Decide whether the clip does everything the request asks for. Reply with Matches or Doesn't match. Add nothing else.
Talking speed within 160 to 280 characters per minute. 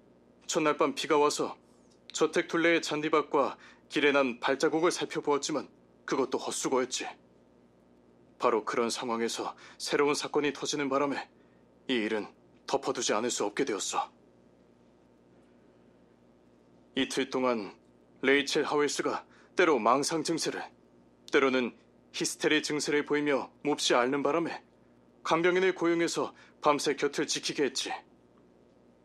Matches